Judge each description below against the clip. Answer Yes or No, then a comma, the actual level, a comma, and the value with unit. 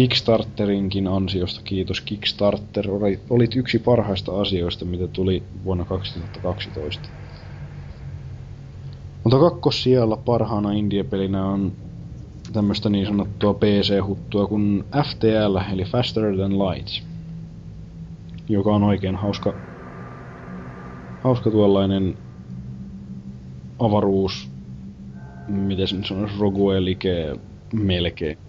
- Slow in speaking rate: Yes, slow, 85 wpm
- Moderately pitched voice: No, low, 100 Hz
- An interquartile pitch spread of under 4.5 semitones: Yes, average, 2.9 semitones